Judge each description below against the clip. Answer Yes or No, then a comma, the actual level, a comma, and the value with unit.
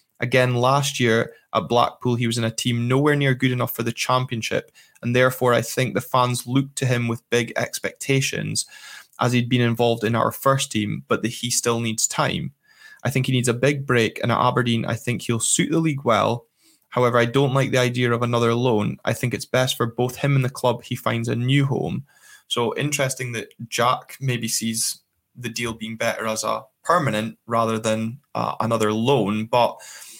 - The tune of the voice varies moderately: No, narrow, 2.2 semitones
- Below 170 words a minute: No, fast, 205 wpm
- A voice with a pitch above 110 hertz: Yes, low, 120 Hz